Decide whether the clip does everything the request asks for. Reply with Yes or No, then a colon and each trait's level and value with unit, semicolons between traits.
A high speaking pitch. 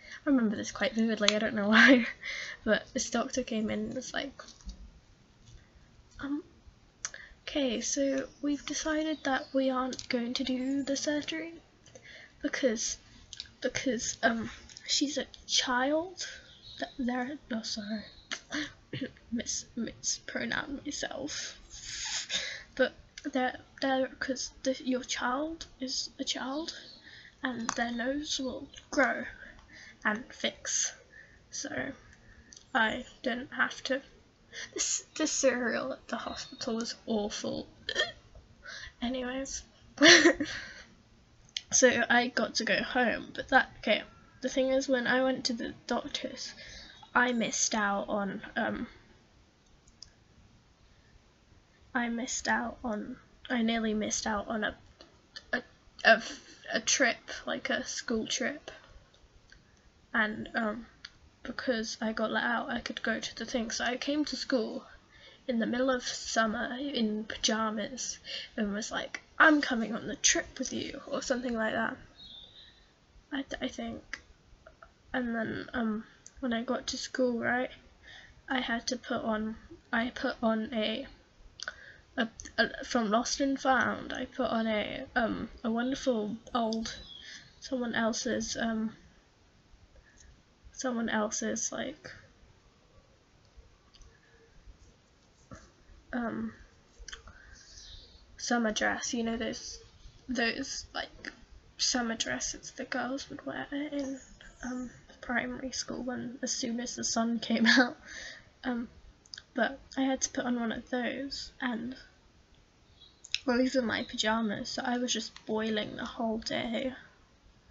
Yes: very high, 250 Hz